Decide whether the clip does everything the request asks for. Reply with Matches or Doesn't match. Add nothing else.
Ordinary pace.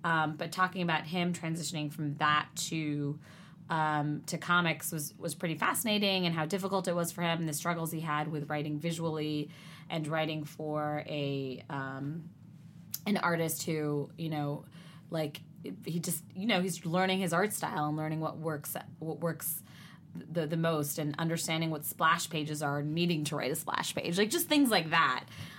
Matches